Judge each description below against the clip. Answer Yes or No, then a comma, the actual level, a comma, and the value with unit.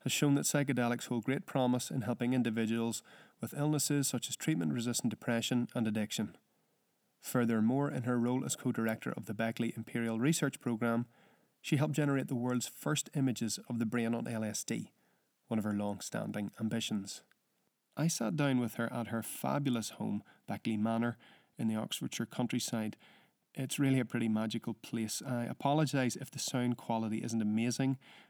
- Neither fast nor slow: Yes, average, 170 wpm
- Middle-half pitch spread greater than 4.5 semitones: No, average, 2.7 semitones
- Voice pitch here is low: Yes, low, 120 Hz